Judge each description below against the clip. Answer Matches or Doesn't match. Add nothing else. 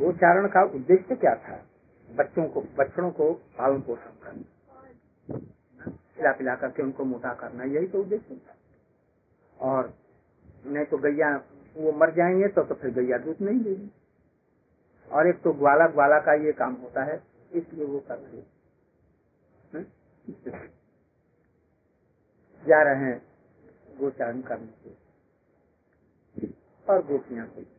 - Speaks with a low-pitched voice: Doesn't match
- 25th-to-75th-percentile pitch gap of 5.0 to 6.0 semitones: Matches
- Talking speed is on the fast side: Doesn't match